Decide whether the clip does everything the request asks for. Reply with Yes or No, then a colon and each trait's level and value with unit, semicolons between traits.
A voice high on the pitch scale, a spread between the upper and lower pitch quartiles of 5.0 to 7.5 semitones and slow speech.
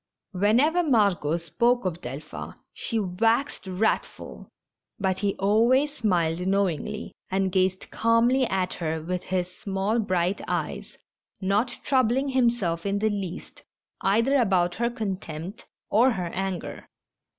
No: high, 195 Hz; average, 4.1 semitones; slow, 130 wpm